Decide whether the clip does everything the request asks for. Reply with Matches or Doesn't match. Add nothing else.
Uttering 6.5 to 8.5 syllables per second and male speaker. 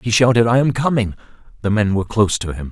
Matches